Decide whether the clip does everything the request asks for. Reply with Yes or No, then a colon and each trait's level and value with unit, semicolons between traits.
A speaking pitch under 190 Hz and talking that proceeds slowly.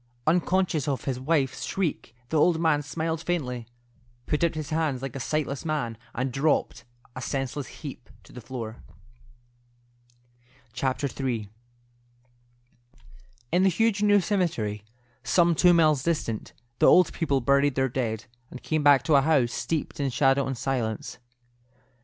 No: medium, 140 Hz; average, 145 wpm